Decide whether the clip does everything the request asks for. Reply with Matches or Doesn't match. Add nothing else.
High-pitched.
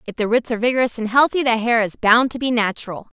Matches